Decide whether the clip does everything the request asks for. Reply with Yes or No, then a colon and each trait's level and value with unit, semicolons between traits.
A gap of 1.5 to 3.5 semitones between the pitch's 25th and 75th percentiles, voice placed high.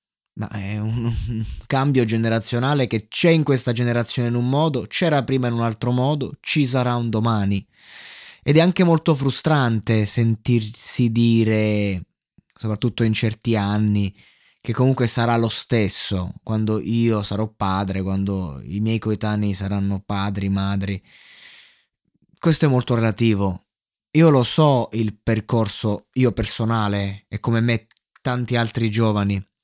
No: average, 3.0 semitones; low, 115 Hz